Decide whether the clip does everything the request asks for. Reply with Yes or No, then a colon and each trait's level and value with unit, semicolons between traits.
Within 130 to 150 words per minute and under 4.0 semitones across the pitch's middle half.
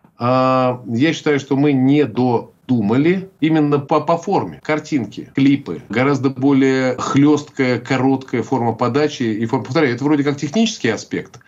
Yes: average, 135 wpm; average, 2.9 semitones